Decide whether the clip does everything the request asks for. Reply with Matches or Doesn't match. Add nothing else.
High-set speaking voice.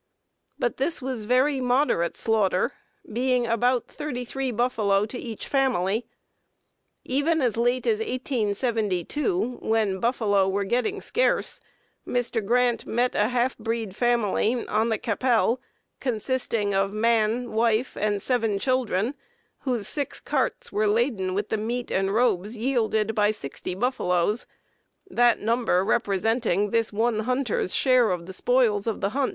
Matches